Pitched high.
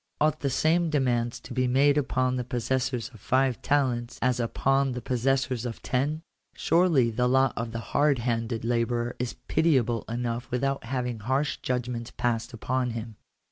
No: low, 125 Hz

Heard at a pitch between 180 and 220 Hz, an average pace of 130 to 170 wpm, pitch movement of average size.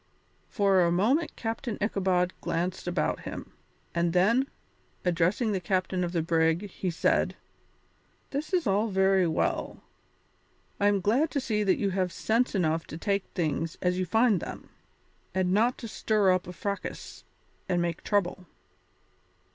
Yes: high, 190 Hz; average, 155 wpm; average, 3.2 semitones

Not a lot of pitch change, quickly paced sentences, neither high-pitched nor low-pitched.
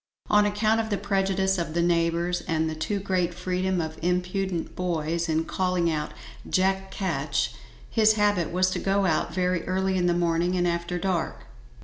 No: narrow, 2.2 semitones; average, 175 wpm; medium, 180 Hz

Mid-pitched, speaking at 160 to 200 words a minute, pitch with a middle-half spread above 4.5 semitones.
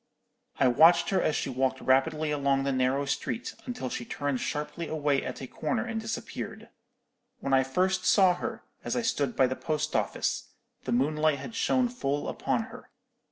Yes: medium, 145 Hz; average, 180 wpm; average, 5.0 semitones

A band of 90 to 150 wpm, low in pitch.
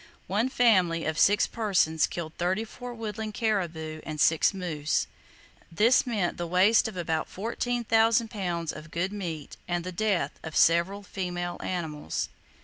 No: average, 145 wpm; medium, 180 Hz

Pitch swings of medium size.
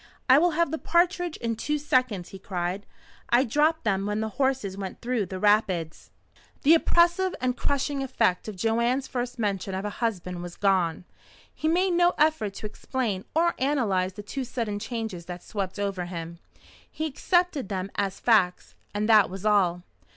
No: wide, 6.3 semitones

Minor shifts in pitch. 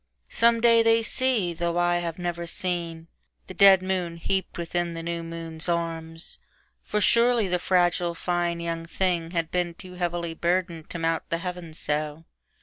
Yes: narrow, 1.7 semitones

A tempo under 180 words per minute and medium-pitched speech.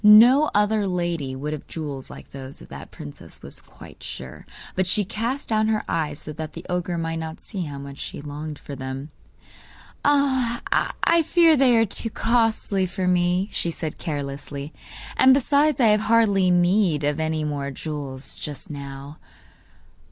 Yes: average, 170 wpm; medium, 175 Hz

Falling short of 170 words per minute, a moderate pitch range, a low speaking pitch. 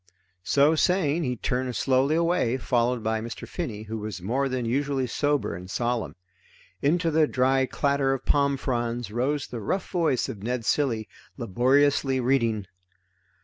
Yes: average, 150 wpm; average, 3.4 semitones; low, 130 Hz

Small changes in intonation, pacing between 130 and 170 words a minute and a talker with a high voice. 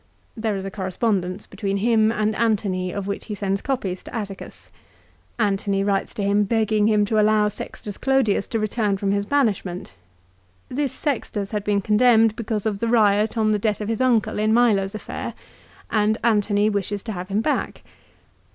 No: narrow, 2.0 semitones; average, 180 wpm; high, 210 Hz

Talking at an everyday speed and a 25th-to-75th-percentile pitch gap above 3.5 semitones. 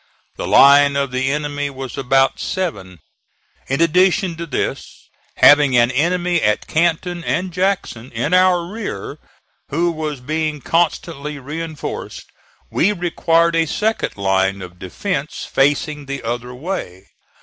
No: slow, 130 wpm; average, 4.6 semitones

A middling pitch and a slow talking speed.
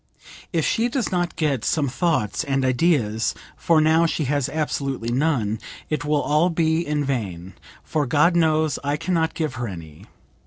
No: medium, 150 Hz; average, 170 wpm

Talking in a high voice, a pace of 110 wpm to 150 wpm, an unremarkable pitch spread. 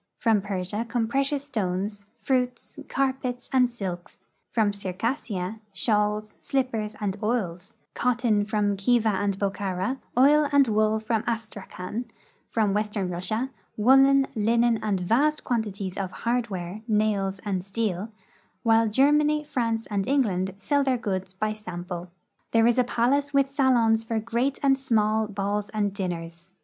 Yes: high, 215 Hz; average, 140 wpm; average, 3.9 semitones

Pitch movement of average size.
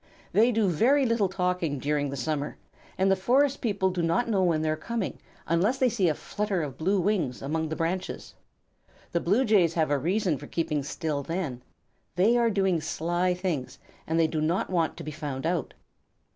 Yes: average, 4.5 semitones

